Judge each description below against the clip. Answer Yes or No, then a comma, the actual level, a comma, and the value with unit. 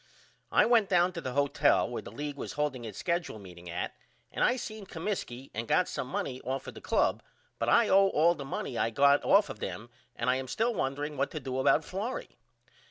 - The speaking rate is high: Yes, fast, 225 wpm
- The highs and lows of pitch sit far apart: Yes, wide, 6.1 semitones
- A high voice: No, medium, 140 Hz